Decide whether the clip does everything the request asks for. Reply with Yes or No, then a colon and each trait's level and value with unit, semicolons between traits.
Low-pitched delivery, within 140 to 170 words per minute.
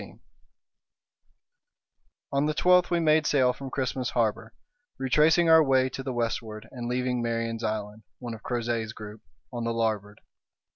Yes: low, 120 Hz; average, 155 wpm